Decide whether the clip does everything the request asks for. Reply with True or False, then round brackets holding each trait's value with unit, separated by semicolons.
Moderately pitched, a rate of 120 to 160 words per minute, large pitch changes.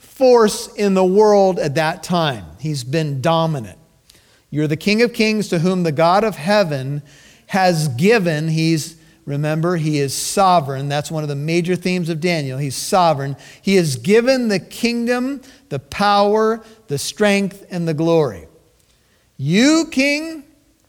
True (170 Hz; 150 wpm; 5.9 semitones)